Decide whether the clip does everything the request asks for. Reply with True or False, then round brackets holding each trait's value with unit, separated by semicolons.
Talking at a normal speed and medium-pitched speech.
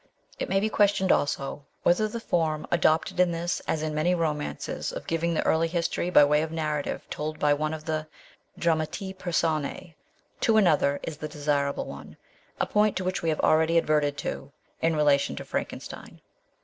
True (180 wpm; 160 Hz)